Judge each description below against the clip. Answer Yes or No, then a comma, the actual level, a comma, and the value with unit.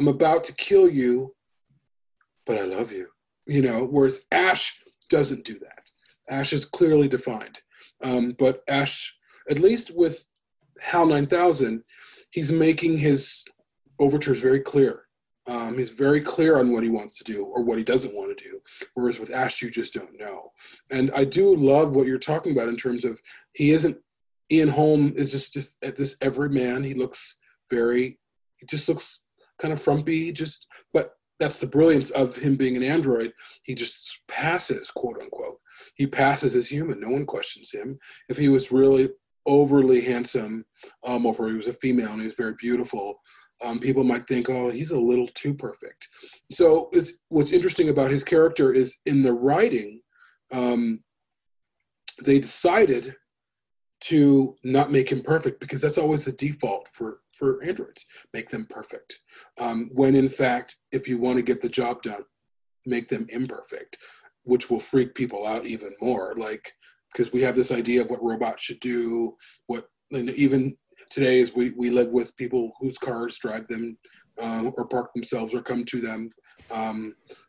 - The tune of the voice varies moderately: Yes, average, 3.5 semitones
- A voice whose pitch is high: No, low, 130 Hz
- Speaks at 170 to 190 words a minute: Yes, average, 175 wpm